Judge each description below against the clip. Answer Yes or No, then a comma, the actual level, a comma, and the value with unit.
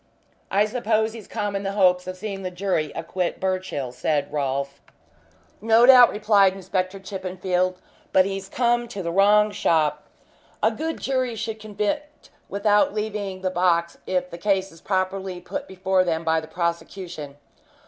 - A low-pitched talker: No, high, 190 Hz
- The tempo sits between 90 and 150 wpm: No, average, 160 wpm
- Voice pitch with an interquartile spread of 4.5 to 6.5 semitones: No, average, 2.9 semitones